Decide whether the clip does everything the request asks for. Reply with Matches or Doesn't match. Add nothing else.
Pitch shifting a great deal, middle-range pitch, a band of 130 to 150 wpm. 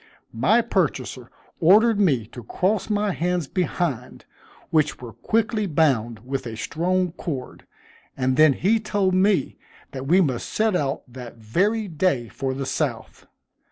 Matches